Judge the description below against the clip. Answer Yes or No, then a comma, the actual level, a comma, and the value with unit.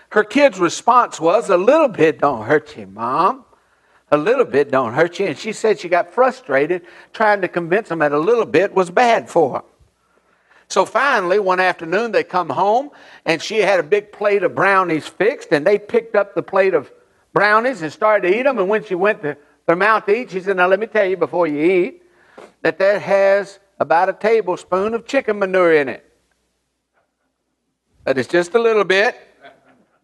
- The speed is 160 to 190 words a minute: No, average, 200 wpm